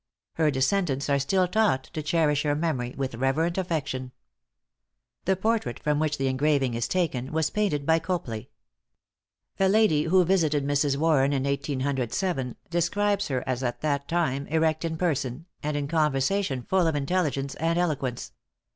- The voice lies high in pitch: No, medium, 150 Hz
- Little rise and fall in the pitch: No, average, 4.2 semitones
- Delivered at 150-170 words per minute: Yes, average, 155 wpm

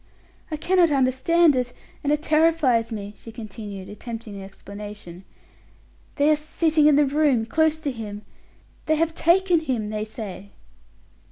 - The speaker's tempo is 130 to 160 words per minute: Yes, average, 150 wpm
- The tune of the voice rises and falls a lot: Yes, wide, 6.7 semitones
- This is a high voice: Yes, very high, 260 Hz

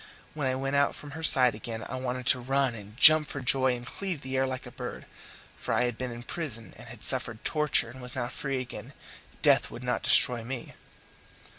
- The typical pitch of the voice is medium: No, low, 130 Hz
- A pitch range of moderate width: No, narrow, 2.3 semitones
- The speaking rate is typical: No, fast, 225 wpm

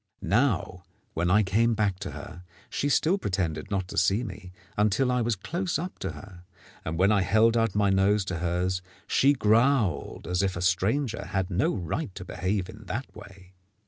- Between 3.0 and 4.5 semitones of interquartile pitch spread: Yes, average, 3.7 semitones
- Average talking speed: Yes, average, 190 wpm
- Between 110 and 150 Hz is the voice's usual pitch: No, low, 100 Hz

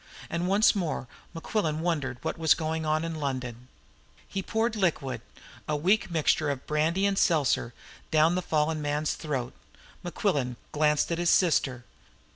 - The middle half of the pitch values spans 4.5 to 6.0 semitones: No, average, 3.1 semitones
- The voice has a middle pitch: Yes, medium, 155 Hz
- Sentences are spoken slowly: No, average, 155 wpm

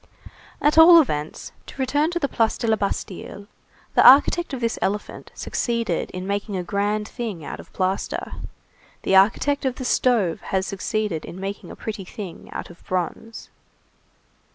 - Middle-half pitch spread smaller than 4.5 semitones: No, average, 4.9 semitones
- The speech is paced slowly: No, average, 165 wpm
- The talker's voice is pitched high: Yes, high, 210 Hz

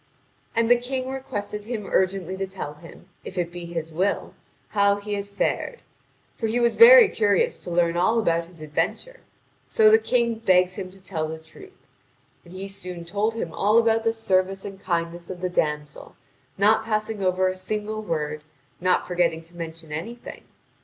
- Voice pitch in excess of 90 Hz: Yes, high, 190 Hz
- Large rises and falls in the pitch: No, average, 4.4 semitones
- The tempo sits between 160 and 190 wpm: Yes, average, 180 wpm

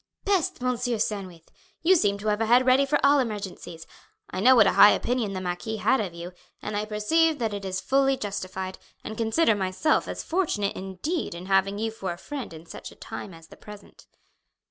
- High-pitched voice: Yes, high, 210 Hz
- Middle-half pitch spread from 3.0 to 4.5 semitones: No, average, 5.1 semitones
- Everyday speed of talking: No, fast, 210 wpm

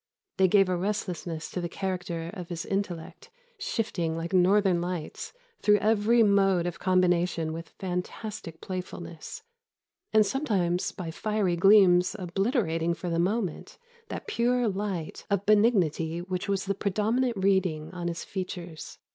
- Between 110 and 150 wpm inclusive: Yes, average, 140 wpm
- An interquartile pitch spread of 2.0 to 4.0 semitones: Yes, average, 3.1 semitones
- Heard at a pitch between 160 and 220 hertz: Yes, medium, 185 Hz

